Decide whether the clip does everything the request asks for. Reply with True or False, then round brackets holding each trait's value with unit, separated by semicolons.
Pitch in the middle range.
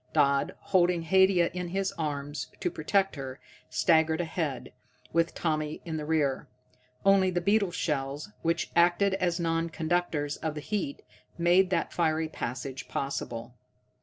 True (165 Hz)